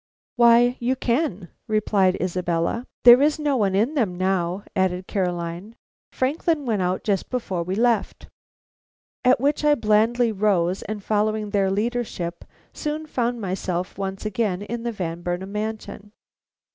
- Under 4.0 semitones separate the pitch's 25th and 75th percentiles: No, average, 4.4 semitones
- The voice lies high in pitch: Yes, high, 210 Hz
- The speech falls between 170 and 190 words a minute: No, average, 145 wpm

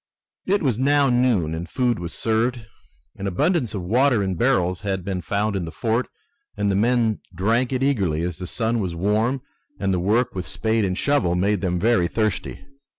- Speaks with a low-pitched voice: Yes, low, 105 Hz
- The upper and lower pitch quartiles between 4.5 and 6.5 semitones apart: Yes, average, 4.9 semitones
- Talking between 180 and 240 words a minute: Yes, average, 195 wpm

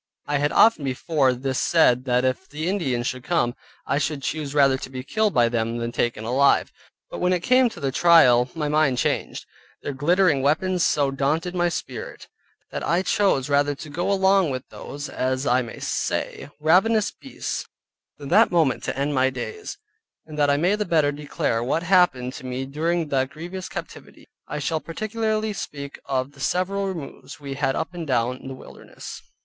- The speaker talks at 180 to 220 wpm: Yes, average, 190 wpm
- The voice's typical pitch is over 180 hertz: No, medium, 145 Hz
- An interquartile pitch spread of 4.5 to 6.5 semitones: Yes, average, 4.9 semitones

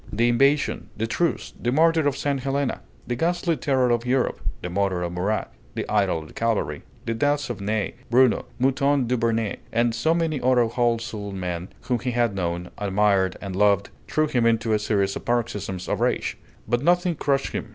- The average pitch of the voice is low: Yes, low, 115 Hz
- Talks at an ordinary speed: Yes, average, 195 wpm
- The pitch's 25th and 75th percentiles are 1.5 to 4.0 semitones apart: No, average, 5.1 semitones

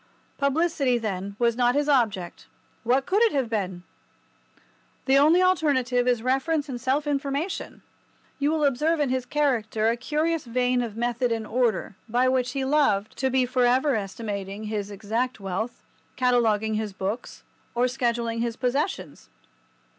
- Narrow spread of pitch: No, average, 4.0 semitones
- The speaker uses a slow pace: No, average, 155 wpm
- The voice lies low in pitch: No, very high, 250 Hz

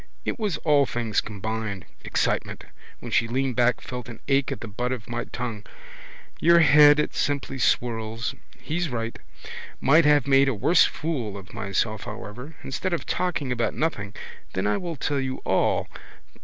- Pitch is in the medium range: No, low, 125 Hz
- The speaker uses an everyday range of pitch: Yes, average, 4.7 semitones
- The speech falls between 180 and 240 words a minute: No, average, 170 wpm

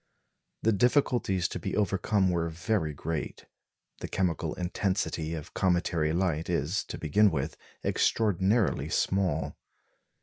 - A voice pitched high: No, very low, 90 Hz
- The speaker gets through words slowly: Yes, slow, 115 wpm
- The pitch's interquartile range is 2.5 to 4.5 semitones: Yes, average, 3.8 semitones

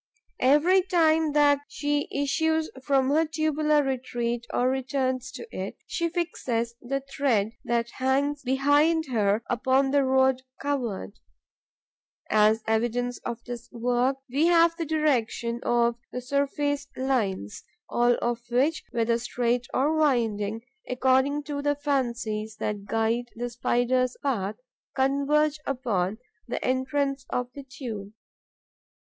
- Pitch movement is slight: No, average, 3.3 semitones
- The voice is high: Yes, very high, 260 Hz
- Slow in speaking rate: Yes, slow, 125 wpm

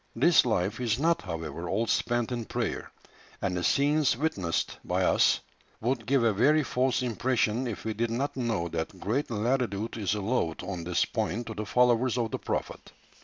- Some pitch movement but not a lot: Yes, average, 4.3 semitones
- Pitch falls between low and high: No, low, 115 Hz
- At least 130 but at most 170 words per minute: No, average, 180 wpm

